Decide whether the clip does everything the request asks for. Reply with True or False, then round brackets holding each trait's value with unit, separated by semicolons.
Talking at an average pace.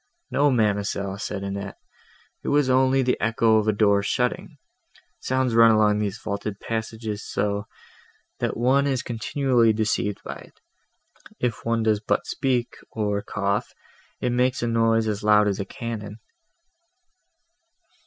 True (145 wpm)